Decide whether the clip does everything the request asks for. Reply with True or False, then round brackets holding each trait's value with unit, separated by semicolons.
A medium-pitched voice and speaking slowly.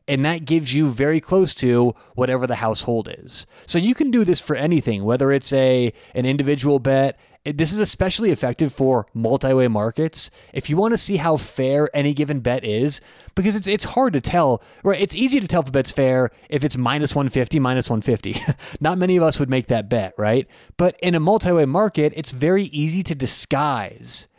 False (145 Hz; 200 wpm)